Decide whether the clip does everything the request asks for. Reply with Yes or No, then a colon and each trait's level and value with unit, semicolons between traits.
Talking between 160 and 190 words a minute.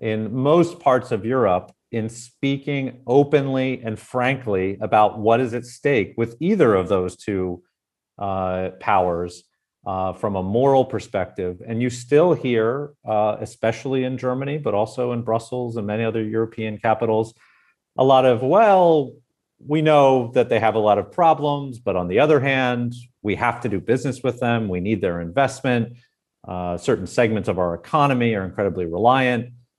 Yes: average, 165 wpm